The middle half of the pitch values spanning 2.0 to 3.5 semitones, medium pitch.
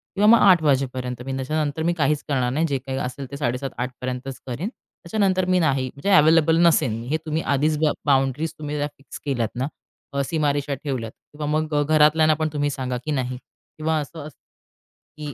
Yes: average, 2.9 semitones; medium, 145 Hz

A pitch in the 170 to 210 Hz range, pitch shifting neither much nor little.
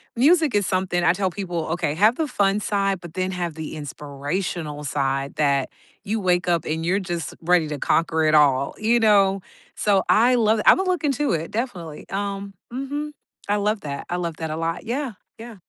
Yes: medium, 185 Hz; average, 5.0 semitones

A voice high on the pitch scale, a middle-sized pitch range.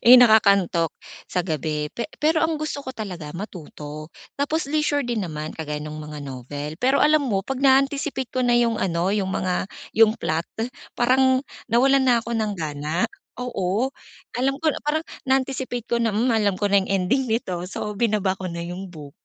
No: high, 215 Hz; wide, 7.4 semitones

